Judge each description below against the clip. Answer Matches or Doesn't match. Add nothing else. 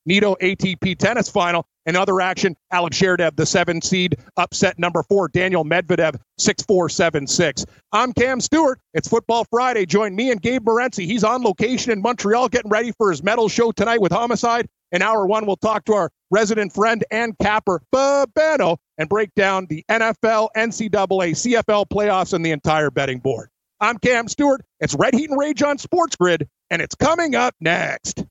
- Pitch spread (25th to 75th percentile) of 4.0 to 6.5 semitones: Matches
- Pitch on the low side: Doesn't match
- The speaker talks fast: Doesn't match